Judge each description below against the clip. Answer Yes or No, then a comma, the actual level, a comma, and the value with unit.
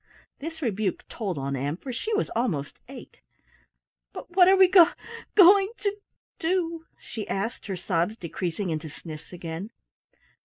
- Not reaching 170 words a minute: Yes, average, 150 wpm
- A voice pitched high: Yes, high, 215 Hz